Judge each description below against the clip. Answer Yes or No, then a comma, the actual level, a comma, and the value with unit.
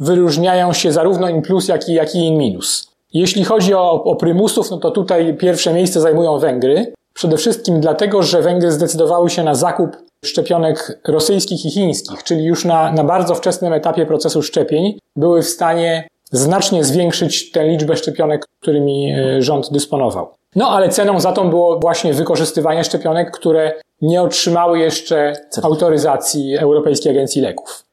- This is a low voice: No, medium, 165 Hz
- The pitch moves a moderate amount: No, narrow, 2.2 semitones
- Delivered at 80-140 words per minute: No, average, 155 wpm